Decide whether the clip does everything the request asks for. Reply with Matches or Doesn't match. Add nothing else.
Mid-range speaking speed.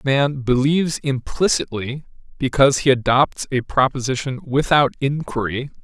Doesn't match